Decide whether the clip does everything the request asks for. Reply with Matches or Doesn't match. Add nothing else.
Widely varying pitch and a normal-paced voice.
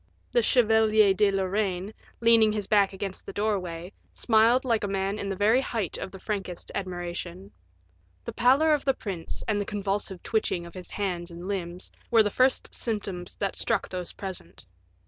Doesn't match